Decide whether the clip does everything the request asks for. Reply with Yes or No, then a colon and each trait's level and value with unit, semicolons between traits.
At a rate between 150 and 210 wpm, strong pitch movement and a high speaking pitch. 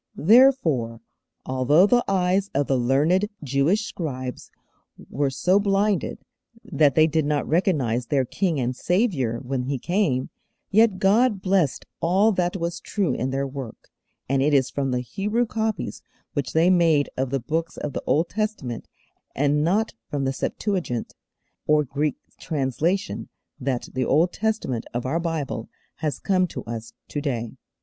No: average, 155 wpm; wide, 6.3 semitones; medium, 150 Hz